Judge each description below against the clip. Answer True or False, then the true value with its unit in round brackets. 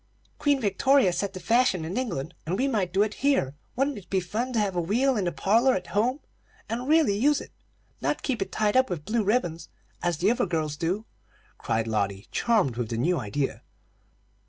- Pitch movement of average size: False (6.5 semitones)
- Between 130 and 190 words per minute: False (205 wpm)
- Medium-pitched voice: False (200 Hz)